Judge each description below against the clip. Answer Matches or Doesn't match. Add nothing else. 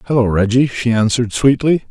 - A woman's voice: Doesn't match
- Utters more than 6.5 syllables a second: Doesn't match